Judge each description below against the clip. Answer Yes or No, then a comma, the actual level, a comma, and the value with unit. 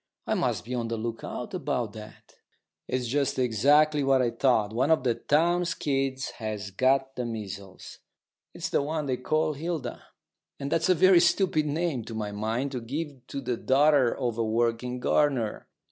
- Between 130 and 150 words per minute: No, average, 175 wpm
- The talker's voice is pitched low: Yes, low, 130 Hz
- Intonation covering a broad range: No, average, 4.3 semitones